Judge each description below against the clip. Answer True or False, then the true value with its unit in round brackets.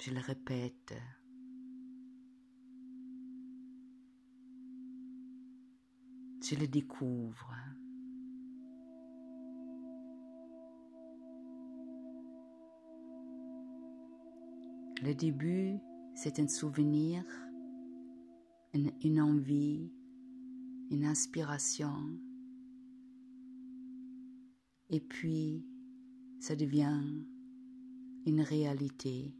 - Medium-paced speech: False (45 wpm)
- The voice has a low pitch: False (150 Hz)